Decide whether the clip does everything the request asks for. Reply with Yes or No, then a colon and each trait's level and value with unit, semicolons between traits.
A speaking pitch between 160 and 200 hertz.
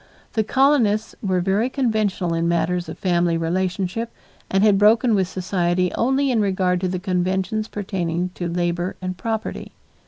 Yes: high, 190 Hz